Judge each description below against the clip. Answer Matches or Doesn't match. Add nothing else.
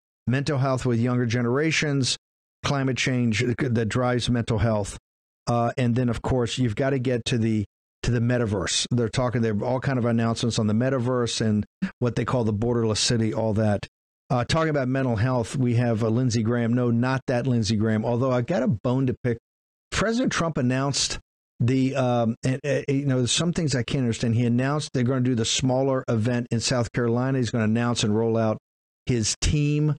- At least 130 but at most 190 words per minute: Doesn't match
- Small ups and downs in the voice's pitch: Matches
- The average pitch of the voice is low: Matches